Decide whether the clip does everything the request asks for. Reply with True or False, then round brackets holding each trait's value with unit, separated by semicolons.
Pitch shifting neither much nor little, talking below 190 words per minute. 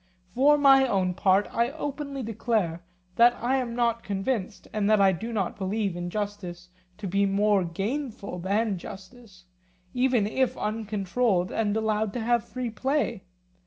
True (3.8 semitones; 150 wpm)